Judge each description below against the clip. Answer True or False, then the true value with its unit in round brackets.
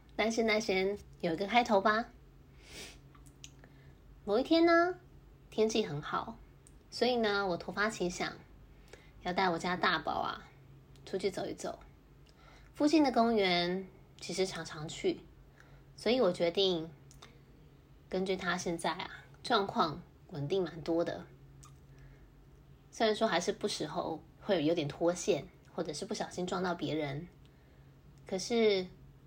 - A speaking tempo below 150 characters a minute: False (190 characters per minute)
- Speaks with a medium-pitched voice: True (180 Hz)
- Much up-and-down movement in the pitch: True (5.7 semitones)